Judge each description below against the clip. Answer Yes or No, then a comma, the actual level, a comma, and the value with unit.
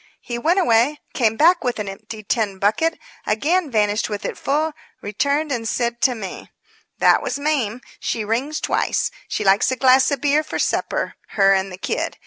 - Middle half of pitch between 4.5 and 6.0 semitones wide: Yes, wide, 5.6 semitones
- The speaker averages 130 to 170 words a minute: No, average, 185 wpm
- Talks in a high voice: Yes, high, 235 Hz